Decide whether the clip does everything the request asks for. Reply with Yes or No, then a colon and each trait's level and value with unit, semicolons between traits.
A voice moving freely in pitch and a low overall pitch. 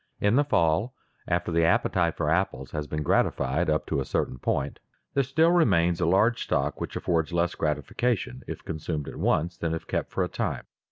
No: average, 4.2 semitones; very low, 85 Hz